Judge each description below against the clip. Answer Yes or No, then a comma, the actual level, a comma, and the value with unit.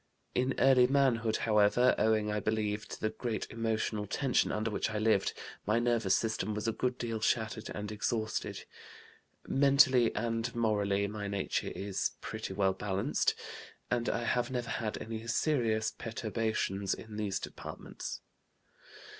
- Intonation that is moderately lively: No, narrow, 2.1 semitones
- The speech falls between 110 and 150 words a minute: Yes, average, 145 wpm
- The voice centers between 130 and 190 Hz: No, low, 110 Hz